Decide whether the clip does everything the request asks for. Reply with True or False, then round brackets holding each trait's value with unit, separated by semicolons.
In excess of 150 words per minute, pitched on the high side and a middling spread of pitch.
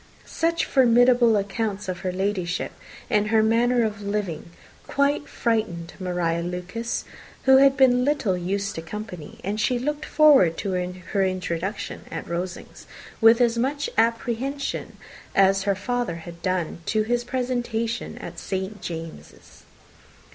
False (135 wpm; 210 Hz; 4.9 semitones)